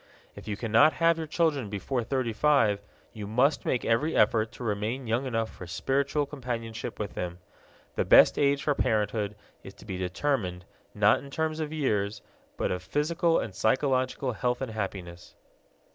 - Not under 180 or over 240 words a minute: No, average, 170 wpm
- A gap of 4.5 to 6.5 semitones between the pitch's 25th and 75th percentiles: Yes, average, 5.1 semitones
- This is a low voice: Yes, low, 120 Hz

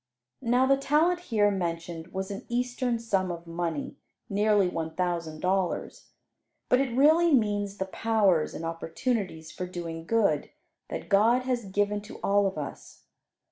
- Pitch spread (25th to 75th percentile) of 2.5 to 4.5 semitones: No, wide, 5.6 semitones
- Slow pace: No, average, 150 wpm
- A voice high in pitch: Yes, high, 200 Hz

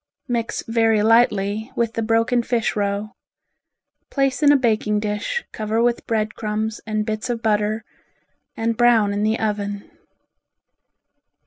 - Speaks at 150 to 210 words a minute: No, slow, 135 wpm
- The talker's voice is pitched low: No, high, 220 Hz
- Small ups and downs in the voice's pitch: Yes, narrow, 1.7 semitones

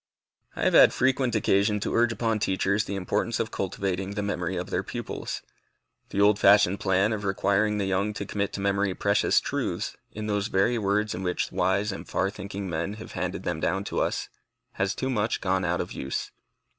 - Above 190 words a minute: Yes, average, 200 wpm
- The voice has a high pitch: No, low, 100 Hz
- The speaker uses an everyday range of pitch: No, narrow, 1.7 semitones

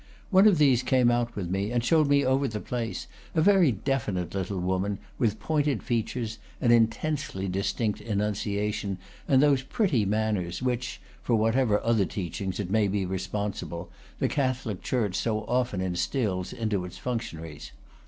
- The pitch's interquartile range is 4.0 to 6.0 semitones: Yes, average, 4.6 semitones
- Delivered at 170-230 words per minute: No, average, 160 wpm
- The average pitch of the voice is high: No, low, 110 Hz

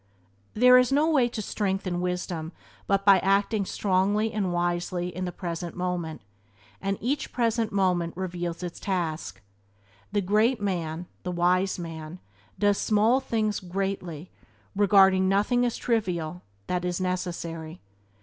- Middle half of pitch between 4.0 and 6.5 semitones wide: No, average, 3.0 semitones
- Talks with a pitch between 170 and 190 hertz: Yes, medium, 185 Hz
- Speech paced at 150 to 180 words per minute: No, average, 140 wpm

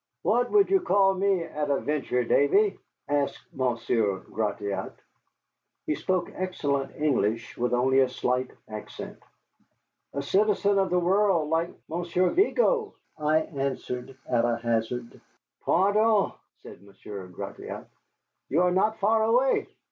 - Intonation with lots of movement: Yes, wide, 7.9 semitones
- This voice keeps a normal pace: No, slow, 130 wpm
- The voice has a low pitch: No, medium, 150 Hz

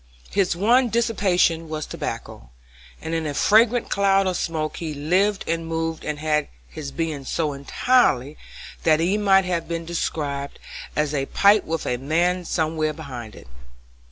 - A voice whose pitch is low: No, medium, 165 Hz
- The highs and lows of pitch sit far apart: No, average, 4.1 semitones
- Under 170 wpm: Yes, average, 155 wpm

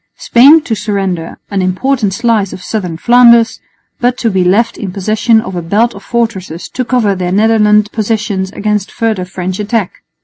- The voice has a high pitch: Yes, high, 210 Hz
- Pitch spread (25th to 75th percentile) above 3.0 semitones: Yes, average, 3.5 semitones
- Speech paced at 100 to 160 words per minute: No, average, 170 wpm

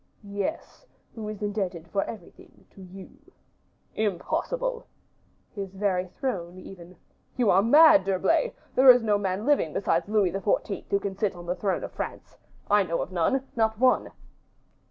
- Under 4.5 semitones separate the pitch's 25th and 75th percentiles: Yes, average, 3.1 semitones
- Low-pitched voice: No, high, 200 Hz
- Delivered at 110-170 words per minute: Yes, average, 155 wpm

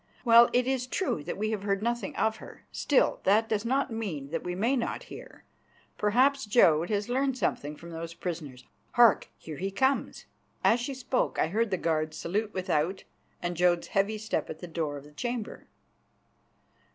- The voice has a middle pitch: No, high, 205 Hz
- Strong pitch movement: Yes, wide, 6.0 semitones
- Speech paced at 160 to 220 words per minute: Yes, average, 180 wpm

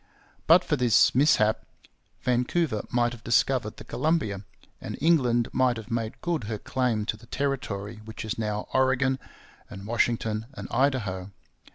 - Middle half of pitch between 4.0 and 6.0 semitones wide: No, average, 3.5 semitones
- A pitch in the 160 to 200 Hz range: No, low, 120 Hz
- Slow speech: No, average, 150 wpm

